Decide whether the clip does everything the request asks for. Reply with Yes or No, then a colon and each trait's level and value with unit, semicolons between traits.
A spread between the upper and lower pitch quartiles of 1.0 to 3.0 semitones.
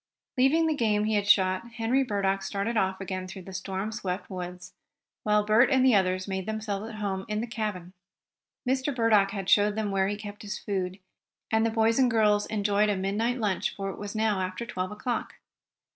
Yes: average, 2.7 semitones